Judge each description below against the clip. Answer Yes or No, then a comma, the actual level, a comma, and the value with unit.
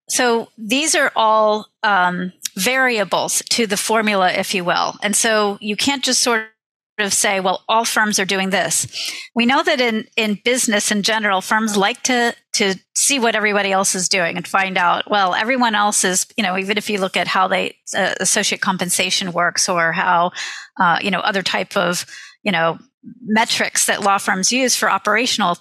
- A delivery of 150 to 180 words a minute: No, average, 190 wpm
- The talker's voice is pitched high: Yes, high, 210 Hz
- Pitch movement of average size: Yes, average, 3.3 semitones